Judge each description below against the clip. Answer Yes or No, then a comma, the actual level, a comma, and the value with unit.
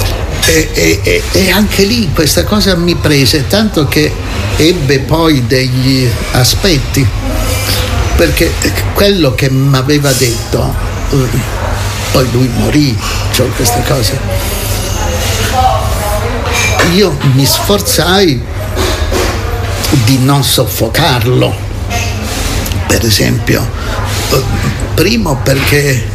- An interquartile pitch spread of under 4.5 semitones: No, average, 5.1 semitones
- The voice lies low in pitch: Yes, low, 105 Hz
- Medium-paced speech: No, slow, 85 wpm